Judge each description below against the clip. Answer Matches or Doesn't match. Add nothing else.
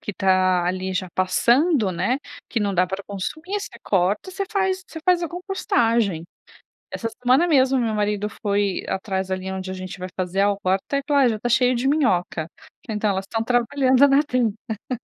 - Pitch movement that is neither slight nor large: Doesn't match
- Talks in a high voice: Matches